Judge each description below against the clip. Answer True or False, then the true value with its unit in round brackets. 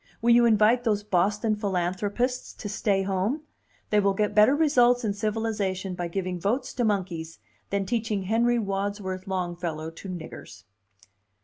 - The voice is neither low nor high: False (205 Hz)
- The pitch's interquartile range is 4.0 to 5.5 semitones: False (3.3 semitones)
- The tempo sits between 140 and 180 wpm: True (145 wpm)